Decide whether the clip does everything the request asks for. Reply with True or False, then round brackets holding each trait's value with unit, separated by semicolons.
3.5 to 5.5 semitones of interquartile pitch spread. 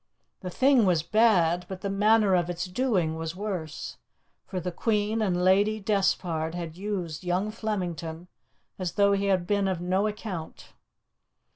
False (3.1 semitones)